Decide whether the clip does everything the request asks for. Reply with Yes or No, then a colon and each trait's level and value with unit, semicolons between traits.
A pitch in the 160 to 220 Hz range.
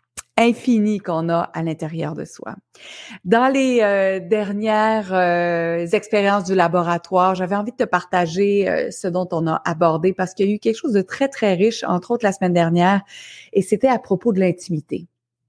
Yes: high, 190 Hz